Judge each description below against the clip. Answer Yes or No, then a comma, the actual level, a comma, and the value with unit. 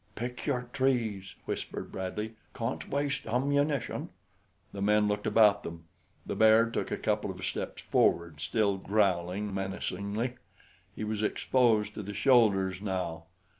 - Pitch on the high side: No, low, 105 Hz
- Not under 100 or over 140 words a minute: Yes, slow, 135 wpm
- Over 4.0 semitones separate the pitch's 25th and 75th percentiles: No, average, 3.5 semitones